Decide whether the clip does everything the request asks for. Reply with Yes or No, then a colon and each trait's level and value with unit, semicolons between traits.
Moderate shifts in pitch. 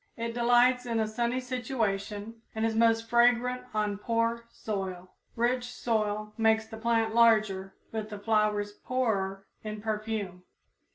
No: narrow, 2.0 semitones